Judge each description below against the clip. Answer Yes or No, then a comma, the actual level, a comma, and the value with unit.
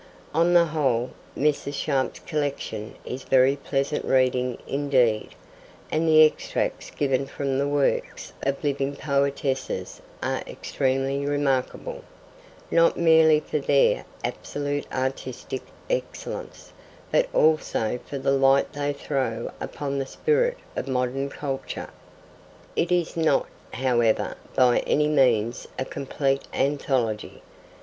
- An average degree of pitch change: No, narrow, 2.0 semitones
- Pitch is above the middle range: No, medium, 140 Hz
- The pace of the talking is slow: Yes, slow, 115 wpm